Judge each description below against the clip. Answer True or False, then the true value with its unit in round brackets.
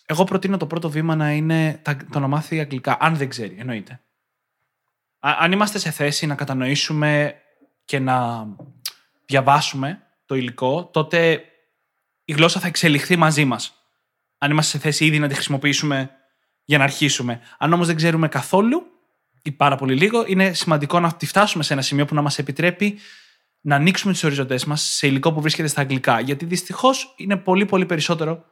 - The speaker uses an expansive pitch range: False (3.5 semitones)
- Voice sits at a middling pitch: True (150 Hz)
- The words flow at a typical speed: False (175 wpm)